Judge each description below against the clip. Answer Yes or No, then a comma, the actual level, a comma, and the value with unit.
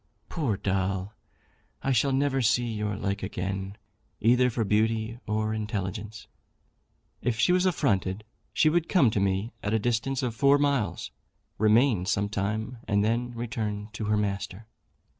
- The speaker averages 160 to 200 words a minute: No, average, 150 wpm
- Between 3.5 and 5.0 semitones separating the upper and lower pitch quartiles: No, average, 3.1 semitones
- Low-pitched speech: Yes, low, 110 Hz